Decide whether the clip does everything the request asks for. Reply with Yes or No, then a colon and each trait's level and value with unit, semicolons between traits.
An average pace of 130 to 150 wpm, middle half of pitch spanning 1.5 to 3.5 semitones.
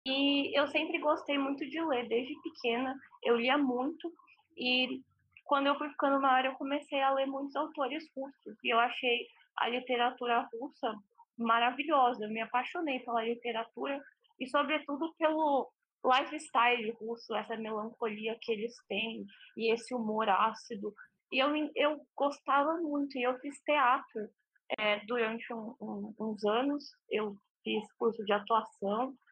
No: average, 145 wpm; average, 4.0 semitones